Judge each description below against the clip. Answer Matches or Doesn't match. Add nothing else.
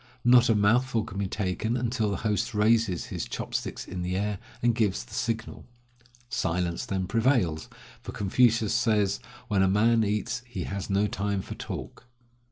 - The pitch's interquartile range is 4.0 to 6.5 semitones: Doesn't match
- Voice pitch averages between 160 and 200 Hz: Doesn't match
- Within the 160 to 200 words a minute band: Matches